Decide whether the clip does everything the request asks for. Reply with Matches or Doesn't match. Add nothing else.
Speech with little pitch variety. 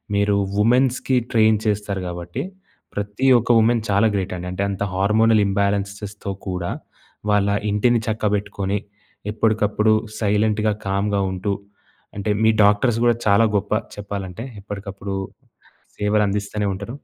Matches